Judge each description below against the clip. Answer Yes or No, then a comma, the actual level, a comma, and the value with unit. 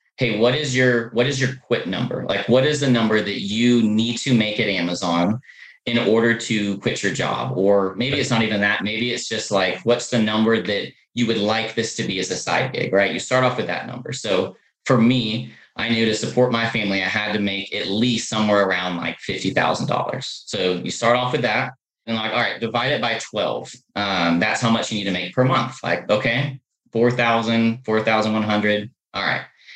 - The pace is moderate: No, fast, 215 wpm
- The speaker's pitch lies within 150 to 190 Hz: No, low, 115 Hz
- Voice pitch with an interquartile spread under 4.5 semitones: Yes, narrow, 2.5 semitones